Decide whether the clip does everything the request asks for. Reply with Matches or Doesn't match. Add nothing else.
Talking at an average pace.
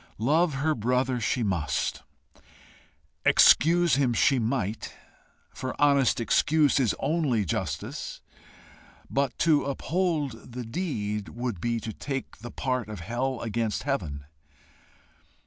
Doesn't match